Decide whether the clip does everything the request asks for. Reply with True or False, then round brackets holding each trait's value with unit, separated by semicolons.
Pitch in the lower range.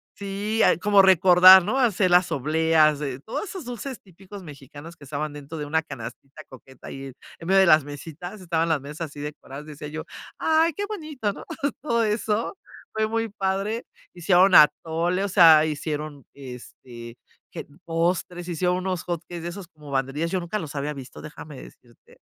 False (170 Hz)